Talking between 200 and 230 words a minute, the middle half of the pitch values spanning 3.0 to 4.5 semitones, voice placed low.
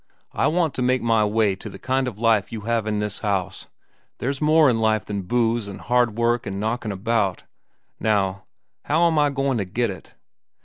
Yes: fast, 205 wpm; average, 3.4 semitones; low, 115 Hz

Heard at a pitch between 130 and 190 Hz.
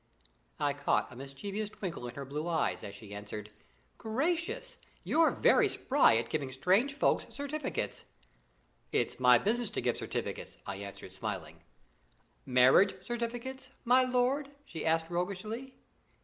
Yes: medium, 185 Hz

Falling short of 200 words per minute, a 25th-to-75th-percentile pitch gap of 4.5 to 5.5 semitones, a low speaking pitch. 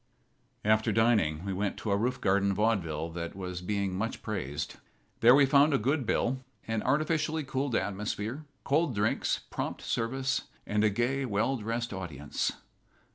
Yes: average, 155 wpm; average, 4.9 semitones; low, 110 Hz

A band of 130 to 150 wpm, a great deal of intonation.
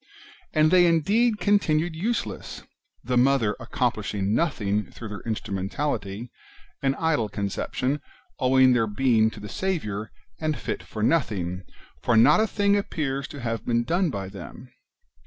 Yes: average, 145 wpm; wide, 7.0 semitones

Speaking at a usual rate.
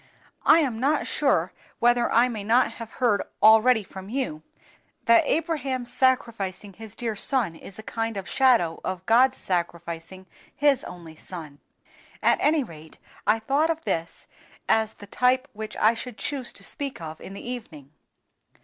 Yes: average, 160 wpm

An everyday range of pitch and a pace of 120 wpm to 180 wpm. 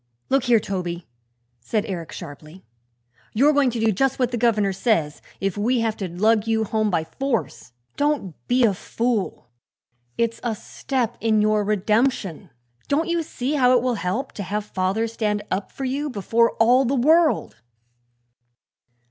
Yes: average, 4.2 semitones; average, 165 wpm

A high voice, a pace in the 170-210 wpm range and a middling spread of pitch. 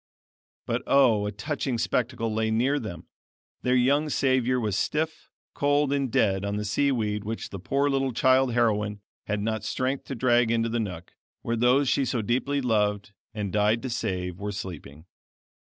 No: low, 115 Hz; average, 175 wpm; average, 4.2 semitones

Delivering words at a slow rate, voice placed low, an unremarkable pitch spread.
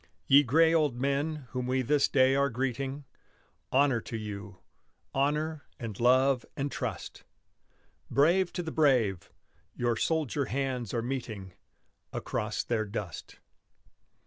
Yes: slow, 125 wpm; low, 130 Hz; average, 3.6 semitones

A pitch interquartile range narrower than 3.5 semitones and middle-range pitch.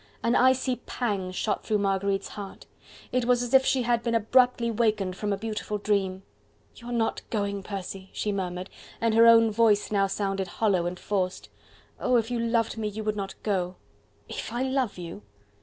No: average, 3.1 semitones; high, 210 Hz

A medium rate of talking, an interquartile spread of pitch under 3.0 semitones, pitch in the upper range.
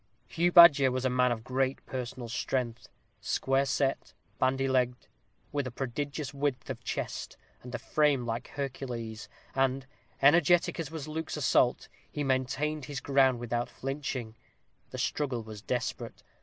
No: average, 150 wpm; narrow, 2.5 semitones; low, 130 Hz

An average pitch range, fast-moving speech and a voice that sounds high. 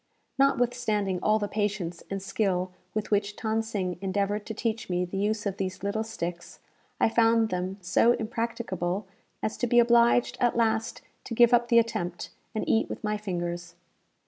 No: average, 3.4 semitones; average, 170 wpm; high, 210 Hz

